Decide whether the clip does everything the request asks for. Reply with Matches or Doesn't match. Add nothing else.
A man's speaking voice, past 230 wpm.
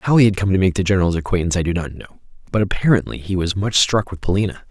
Matches